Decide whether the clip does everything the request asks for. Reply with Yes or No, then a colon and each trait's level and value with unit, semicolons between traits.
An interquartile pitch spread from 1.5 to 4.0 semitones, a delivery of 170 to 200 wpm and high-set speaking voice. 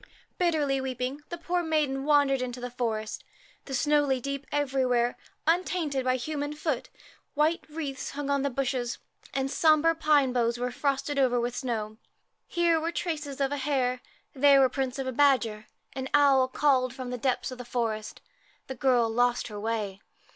Yes: average, 2.8 semitones; average, 180 wpm; very high, 270 Hz